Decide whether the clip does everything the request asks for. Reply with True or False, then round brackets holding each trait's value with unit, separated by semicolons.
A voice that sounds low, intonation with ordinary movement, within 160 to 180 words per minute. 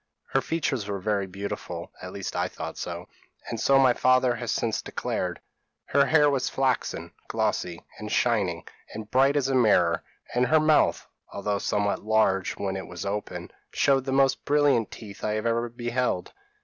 True (115 Hz; 4.8 semitones; 175 wpm)